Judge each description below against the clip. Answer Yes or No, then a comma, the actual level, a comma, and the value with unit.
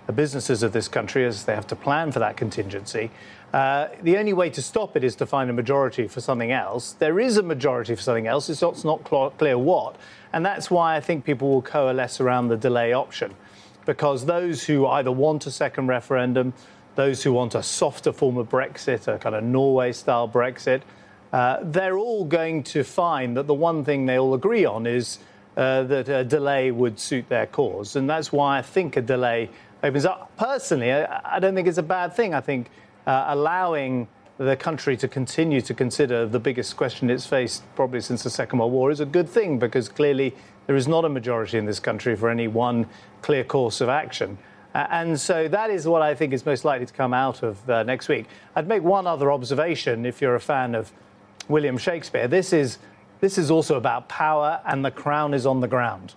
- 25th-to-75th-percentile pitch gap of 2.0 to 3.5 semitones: No, average, 4.0 semitones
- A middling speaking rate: No, fast, 215 wpm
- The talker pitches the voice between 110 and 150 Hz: Yes, low, 135 Hz